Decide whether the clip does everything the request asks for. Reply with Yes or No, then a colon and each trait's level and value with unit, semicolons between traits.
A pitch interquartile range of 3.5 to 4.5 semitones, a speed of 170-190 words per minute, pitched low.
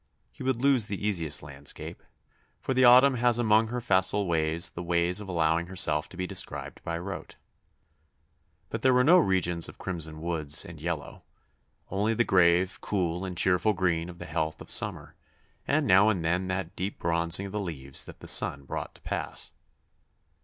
Yes: average, 4.0 semitones; average, 180 wpm; very low, 90 Hz